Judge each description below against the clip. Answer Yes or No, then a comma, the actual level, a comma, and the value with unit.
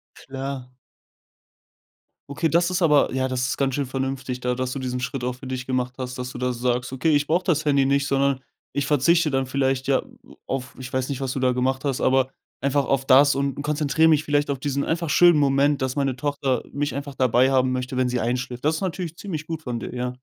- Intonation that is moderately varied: No, narrow, 2.2 semitones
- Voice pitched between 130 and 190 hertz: Yes, low, 135 Hz